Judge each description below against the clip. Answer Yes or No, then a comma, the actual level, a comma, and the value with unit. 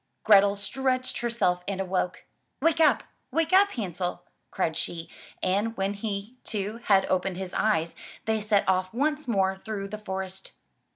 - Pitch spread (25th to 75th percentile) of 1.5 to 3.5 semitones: Yes, average, 3.2 semitones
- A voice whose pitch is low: No, high, 200 Hz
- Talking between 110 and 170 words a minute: Yes, average, 160 wpm